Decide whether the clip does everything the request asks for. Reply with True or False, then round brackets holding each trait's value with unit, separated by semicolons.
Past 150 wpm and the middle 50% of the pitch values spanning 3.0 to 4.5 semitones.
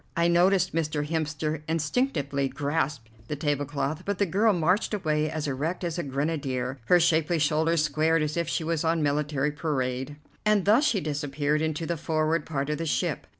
False (180 wpm; 2.4 semitones)